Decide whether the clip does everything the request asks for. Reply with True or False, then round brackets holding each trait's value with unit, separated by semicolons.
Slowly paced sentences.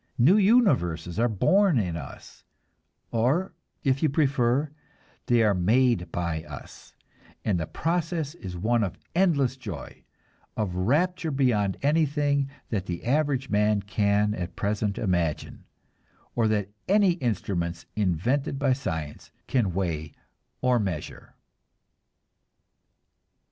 True (115 wpm)